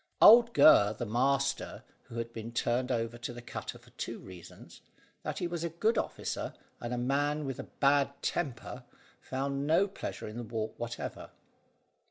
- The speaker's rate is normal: Yes, average, 175 wpm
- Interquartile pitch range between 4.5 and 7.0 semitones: No, average, 3.8 semitones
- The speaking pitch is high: No, low, 130 Hz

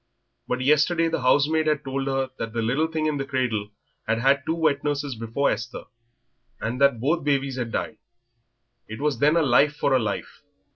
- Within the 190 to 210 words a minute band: Yes, average, 195 wpm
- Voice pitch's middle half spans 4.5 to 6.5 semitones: No, average, 3.3 semitones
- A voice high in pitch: No, low, 135 Hz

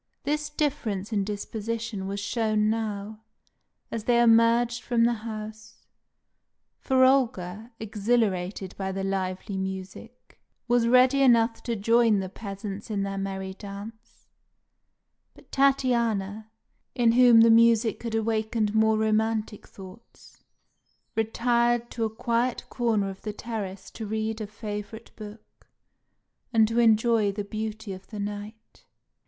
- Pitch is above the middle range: Yes, high, 220 Hz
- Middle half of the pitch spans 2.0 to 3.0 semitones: Yes, narrow, 2.4 semitones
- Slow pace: Yes, slow, 130 wpm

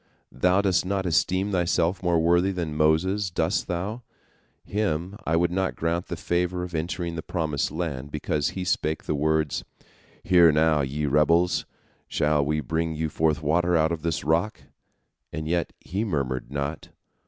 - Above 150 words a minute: Yes, average, 165 wpm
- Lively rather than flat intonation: No, narrow, 2.6 semitones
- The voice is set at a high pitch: No, very low, 85 Hz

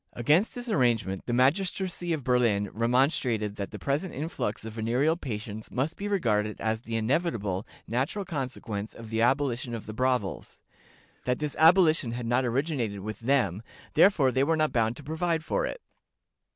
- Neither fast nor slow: Yes, average, 165 wpm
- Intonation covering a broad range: Yes, wide, 5.9 semitones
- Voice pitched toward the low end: Yes, low, 125 Hz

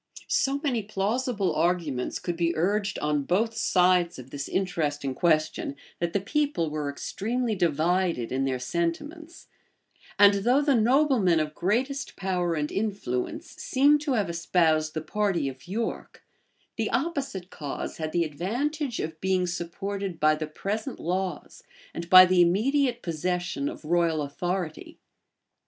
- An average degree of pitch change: No, wide, 5.7 semitones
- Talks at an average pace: Yes, average, 145 wpm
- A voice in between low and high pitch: Yes, medium, 180 Hz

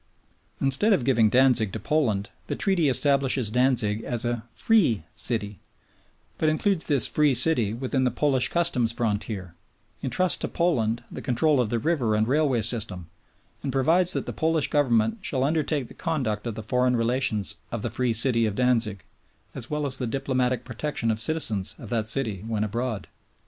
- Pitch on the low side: Yes, low, 125 Hz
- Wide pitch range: No, average, 4.4 semitones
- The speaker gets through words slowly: No, average, 175 wpm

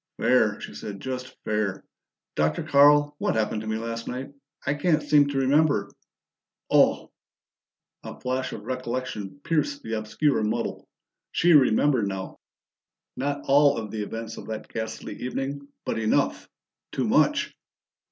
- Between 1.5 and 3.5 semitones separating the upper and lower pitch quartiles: No, average, 4.5 semitones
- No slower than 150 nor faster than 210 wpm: No, average, 140 wpm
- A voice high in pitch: No, low, 125 Hz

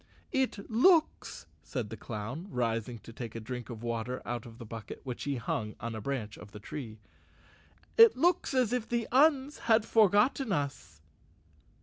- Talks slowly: No, average, 175 wpm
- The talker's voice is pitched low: Yes, low, 130 Hz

